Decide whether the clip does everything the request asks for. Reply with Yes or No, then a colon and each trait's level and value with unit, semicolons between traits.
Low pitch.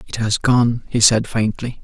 Yes: low, 115 Hz